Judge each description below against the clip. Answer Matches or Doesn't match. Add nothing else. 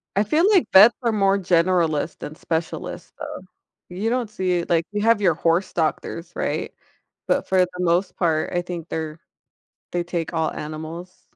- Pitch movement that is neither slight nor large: Matches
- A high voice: Doesn't match